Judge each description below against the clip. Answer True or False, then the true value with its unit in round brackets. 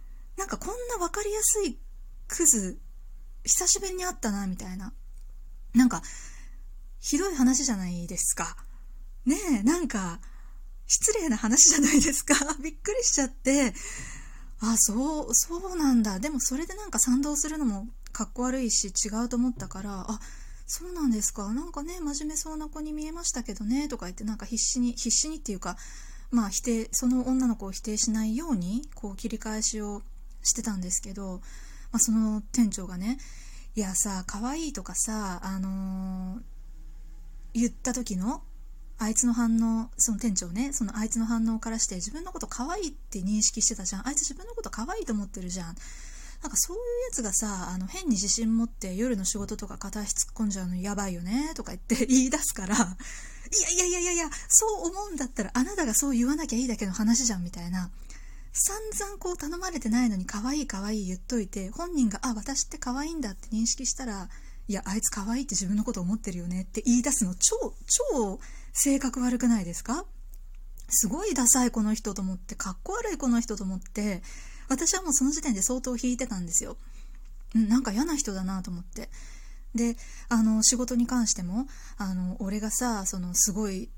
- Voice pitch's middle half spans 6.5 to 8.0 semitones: False (5.3 semitones)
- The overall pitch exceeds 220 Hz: True (230 Hz)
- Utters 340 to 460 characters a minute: True (365 characters per minute)